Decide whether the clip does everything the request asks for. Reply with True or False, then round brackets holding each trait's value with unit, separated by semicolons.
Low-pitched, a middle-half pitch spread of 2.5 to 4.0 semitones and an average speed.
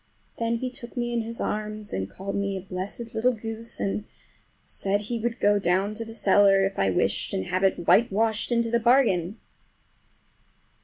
False (215 Hz; 3.1 semitones; 170 wpm)